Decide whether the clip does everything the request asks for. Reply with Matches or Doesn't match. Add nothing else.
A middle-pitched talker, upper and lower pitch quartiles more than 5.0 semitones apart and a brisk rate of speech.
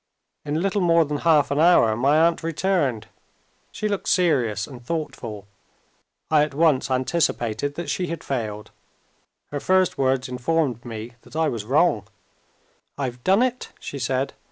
Doesn't match